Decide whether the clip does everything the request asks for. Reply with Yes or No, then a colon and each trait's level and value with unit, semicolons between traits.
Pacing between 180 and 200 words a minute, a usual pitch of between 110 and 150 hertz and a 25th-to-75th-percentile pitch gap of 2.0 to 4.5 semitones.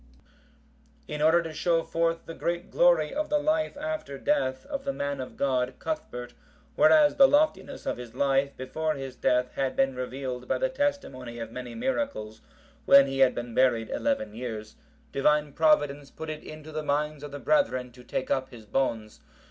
No: average, 185 wpm; medium, 140 Hz; average, 5.2 semitones